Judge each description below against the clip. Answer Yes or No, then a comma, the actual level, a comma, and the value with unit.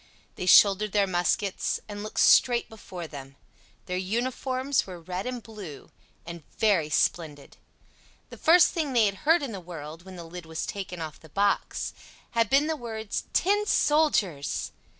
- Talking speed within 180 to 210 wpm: No, average, 165 wpm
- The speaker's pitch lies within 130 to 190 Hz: No, high, 200 Hz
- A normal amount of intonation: No, wide, 5.9 semitones